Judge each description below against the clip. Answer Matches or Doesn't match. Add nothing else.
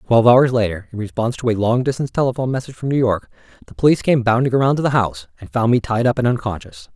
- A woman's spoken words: Doesn't match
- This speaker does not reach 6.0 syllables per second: Doesn't match